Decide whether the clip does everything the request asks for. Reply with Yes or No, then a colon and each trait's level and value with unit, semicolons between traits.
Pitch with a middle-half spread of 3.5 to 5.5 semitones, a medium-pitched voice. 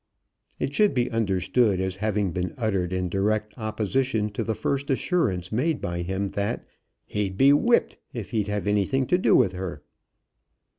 No: average, 4.8 semitones; low, 105 Hz